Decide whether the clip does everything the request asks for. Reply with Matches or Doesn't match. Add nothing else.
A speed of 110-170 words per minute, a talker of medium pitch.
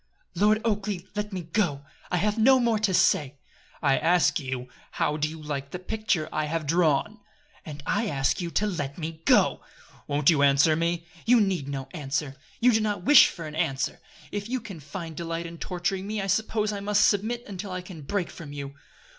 Doesn't match